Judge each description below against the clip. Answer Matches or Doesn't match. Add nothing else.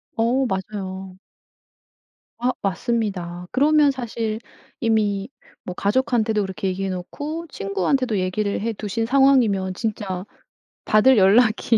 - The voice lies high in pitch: Matches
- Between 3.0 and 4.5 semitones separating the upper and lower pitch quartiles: Matches